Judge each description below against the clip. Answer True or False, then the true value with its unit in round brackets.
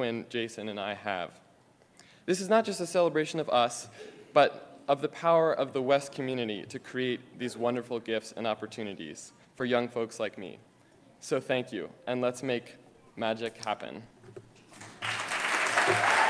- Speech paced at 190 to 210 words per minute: False (145 wpm)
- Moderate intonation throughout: True (3.4 semitones)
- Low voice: True (120 Hz)